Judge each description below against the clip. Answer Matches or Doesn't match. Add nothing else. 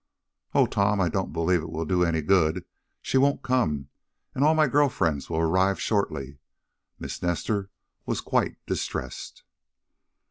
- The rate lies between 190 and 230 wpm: Doesn't match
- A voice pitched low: Matches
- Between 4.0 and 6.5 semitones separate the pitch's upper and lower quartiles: Matches